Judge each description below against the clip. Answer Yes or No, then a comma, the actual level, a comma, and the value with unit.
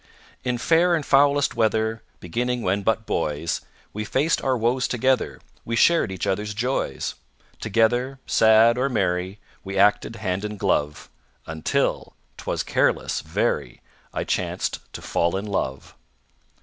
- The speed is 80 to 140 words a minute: Yes, slow, 135 wpm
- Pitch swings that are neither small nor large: Yes, average, 4.4 semitones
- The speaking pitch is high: No, low, 110 Hz